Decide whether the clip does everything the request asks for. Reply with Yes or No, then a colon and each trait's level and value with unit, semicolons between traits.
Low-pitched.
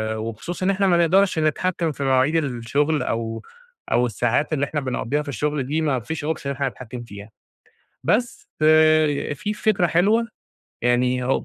No: medium, 145 Hz